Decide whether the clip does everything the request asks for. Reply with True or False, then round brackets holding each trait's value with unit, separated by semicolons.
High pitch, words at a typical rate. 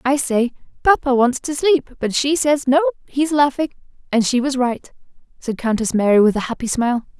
True (265 Hz; 190 wpm)